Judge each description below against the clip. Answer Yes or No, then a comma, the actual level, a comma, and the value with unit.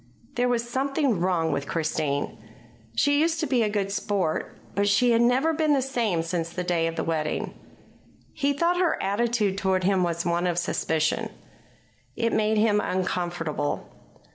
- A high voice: Yes, high, 200 Hz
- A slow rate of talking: No, average, 165 wpm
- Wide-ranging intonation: Yes, wide, 6.4 semitones